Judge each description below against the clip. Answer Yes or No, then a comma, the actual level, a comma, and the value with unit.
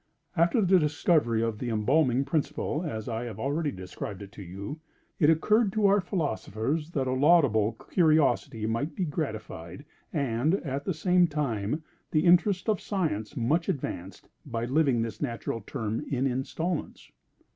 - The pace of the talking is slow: No, average, 155 wpm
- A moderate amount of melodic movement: No, wide, 6.3 semitones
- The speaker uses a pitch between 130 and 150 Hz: Yes, medium, 140 Hz